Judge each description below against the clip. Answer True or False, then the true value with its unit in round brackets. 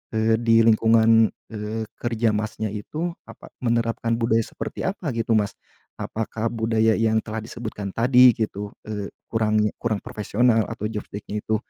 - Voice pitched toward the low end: True (110 Hz)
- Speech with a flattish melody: True (1.2 semitones)